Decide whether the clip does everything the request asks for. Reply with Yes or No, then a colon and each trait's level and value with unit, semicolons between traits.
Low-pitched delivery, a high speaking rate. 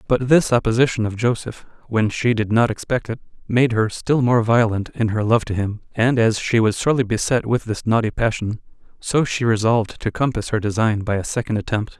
Yes: low, 115 Hz; fast, 210 wpm